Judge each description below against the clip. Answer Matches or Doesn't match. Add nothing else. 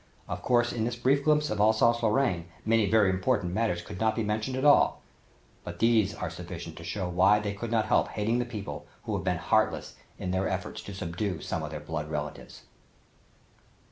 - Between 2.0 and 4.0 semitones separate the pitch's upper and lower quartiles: Doesn't match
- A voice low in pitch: Matches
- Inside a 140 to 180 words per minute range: Doesn't match